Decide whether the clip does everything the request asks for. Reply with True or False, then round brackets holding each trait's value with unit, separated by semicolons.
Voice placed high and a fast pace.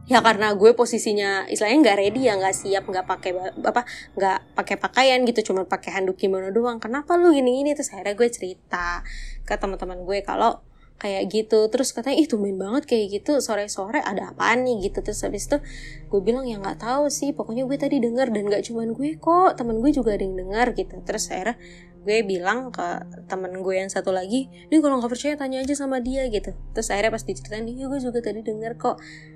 True (220 Hz; 215 wpm)